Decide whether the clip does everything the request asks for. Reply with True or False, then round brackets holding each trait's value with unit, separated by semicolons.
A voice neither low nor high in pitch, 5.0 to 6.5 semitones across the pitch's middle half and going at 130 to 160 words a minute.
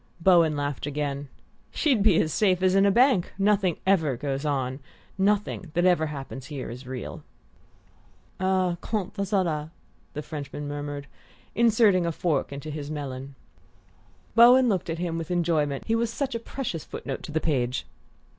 False (165 Hz; 5.3 semitones; 170 wpm)